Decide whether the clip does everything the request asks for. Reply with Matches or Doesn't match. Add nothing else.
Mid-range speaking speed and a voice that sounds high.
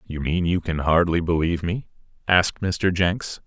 Doesn't match